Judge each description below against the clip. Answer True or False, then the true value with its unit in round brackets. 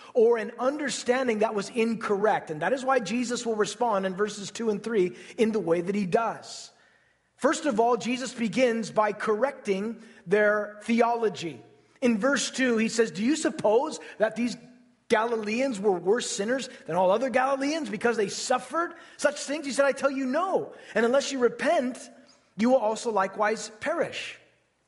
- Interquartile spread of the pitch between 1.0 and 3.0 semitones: False (3.7 semitones)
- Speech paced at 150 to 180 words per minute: True (170 wpm)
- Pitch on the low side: False (230 Hz)